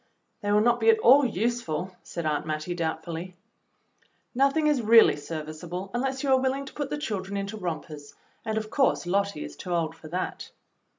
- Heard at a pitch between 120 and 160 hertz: No, high, 200 Hz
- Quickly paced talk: Yes, fast, 215 wpm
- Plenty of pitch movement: Yes, wide, 6.7 semitones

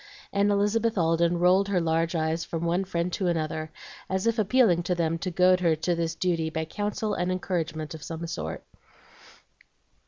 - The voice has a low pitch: No, medium, 170 Hz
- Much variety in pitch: No, narrow, 2.6 semitones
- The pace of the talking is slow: No, average, 180 wpm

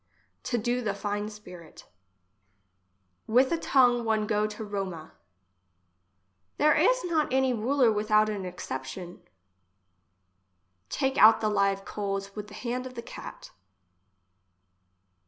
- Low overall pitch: No, high, 215 Hz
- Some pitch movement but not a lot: Yes, average, 3.8 semitones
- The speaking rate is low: Yes, slow, 120 wpm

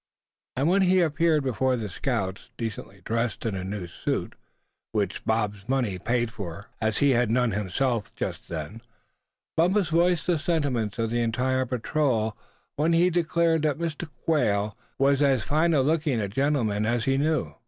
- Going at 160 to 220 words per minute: Yes, average, 165 wpm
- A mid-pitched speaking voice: No, low, 125 Hz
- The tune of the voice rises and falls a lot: Yes, wide, 6.2 semitones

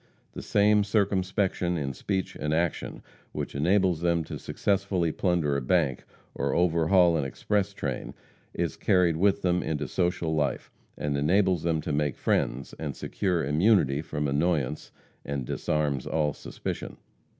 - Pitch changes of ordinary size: Yes, average, 4.2 semitones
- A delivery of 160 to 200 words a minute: No, average, 145 wpm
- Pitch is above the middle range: No, very low, 85 Hz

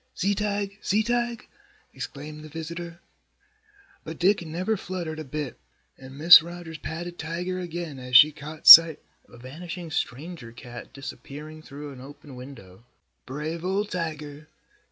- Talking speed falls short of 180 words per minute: Yes, average, 145 wpm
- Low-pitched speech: No, medium, 160 Hz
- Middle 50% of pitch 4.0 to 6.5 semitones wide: No, average, 3.6 semitones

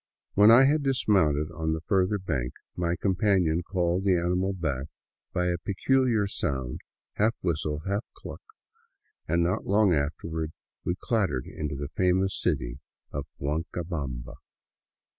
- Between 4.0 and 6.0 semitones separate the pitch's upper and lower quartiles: Yes, average, 4.4 semitones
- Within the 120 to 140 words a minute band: Yes, slow, 135 wpm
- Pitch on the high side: No, very low, 85 Hz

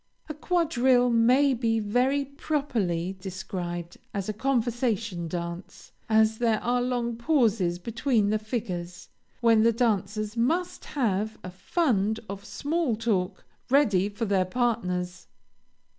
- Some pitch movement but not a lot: Yes, average, 4.5 semitones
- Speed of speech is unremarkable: No, slow, 125 wpm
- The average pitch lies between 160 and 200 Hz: No, high, 225 Hz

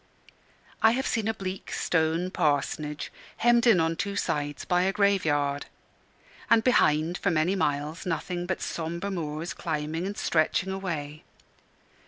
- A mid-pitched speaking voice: Yes, medium, 170 Hz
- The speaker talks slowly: No, average, 145 wpm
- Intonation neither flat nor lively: Yes, average, 4.2 semitones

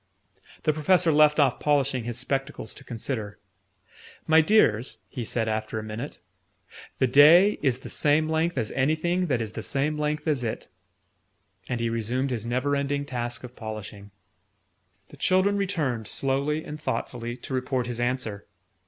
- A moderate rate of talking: Yes, average, 160 wpm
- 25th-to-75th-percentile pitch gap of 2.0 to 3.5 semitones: No, average, 4.3 semitones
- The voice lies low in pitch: Yes, low, 130 Hz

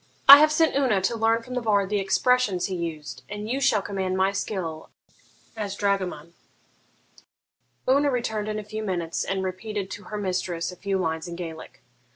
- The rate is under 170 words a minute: No, average, 185 wpm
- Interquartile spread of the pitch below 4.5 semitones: Yes, average, 3.2 semitones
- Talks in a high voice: Yes, high, 200 Hz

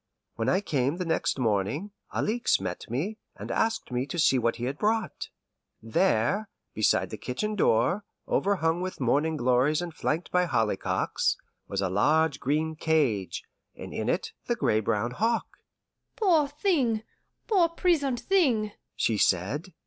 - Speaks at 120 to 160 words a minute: Yes, average, 150 wpm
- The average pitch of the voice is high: No, medium, 160 Hz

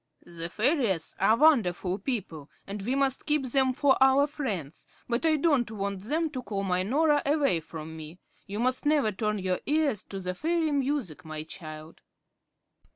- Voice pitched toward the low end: No, high, 225 Hz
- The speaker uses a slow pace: No, average, 170 wpm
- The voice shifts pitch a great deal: Yes, wide, 7.6 semitones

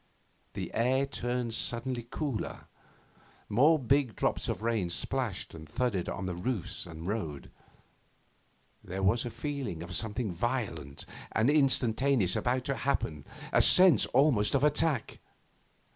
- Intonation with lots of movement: Yes, wide, 5.7 semitones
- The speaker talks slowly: Yes, slow, 130 wpm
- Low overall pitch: Yes, low, 120 Hz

